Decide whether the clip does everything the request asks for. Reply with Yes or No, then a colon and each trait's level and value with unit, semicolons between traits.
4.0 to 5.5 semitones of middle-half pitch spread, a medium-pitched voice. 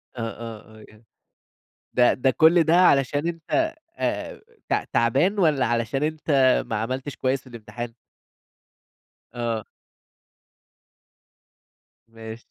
No: average, 4.7 semitones; low, 130 Hz